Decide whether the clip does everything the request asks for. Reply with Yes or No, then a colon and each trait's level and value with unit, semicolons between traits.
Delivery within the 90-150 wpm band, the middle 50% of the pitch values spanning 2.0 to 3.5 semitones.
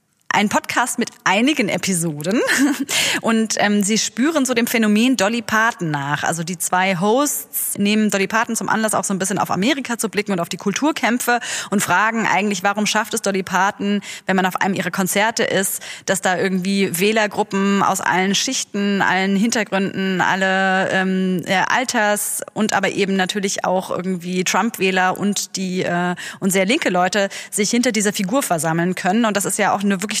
No: average, 180 wpm; average, 3.0 semitones